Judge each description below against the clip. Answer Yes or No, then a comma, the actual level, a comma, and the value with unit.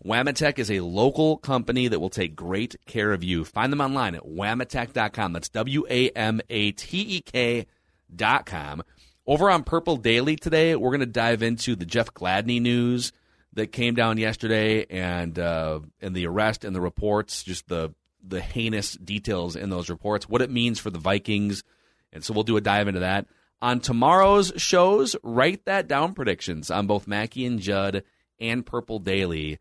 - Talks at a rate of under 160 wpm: No, average, 170 wpm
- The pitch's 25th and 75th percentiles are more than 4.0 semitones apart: Yes, average, 4.6 semitones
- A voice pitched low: Yes, low, 110 Hz